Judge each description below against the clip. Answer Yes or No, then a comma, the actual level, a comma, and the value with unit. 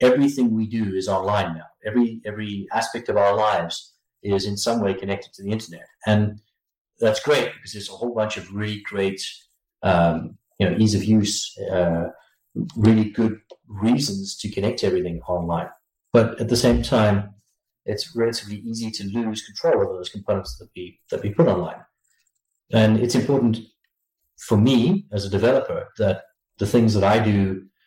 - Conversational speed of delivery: Yes, average, 170 wpm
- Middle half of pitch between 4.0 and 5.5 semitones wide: No, narrow, 2.6 semitones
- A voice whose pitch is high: No, low, 105 Hz